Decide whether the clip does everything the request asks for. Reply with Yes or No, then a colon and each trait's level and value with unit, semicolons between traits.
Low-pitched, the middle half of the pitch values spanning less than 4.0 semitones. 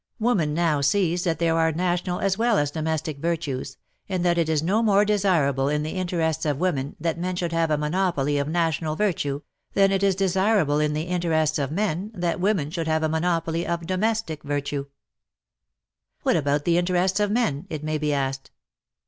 No: medium, 165 Hz; average, 3.5 semitones